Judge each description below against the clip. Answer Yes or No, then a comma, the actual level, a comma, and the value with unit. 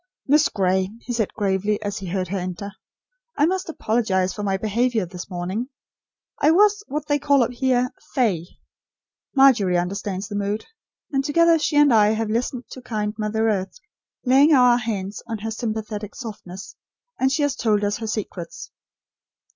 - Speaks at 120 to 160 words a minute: No, average, 170 wpm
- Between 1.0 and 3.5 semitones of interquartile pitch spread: No, average, 4.8 semitones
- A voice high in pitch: Yes, high, 220 Hz